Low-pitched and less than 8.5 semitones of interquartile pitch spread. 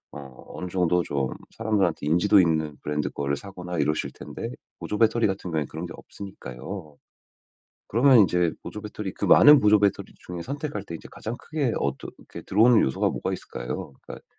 Yes: very low, 90 Hz; wide, 5.5 semitones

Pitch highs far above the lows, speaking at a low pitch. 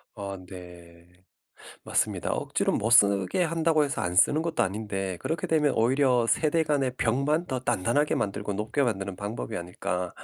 Yes: wide, 7.1 semitones; low, 115 Hz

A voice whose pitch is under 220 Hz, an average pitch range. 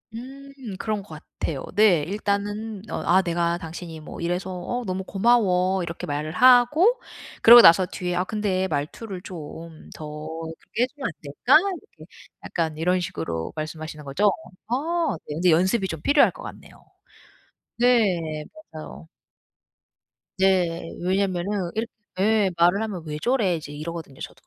Yes: medium, 185 Hz; average, 4.9 semitones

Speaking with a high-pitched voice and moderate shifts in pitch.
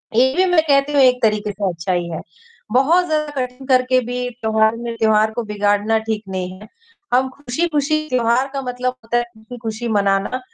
Yes: high, 240 Hz; average, 3.5 semitones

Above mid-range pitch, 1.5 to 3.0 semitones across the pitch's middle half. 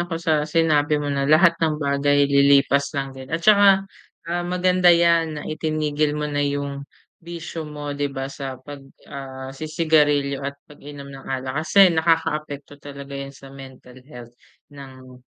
No: medium, 145 Hz; narrow, 2.5 semitones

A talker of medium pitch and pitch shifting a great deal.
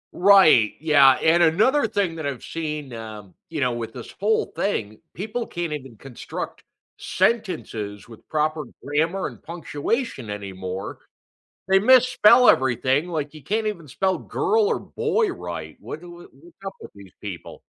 Yes: medium, 155 Hz; wide, 8.0 semitones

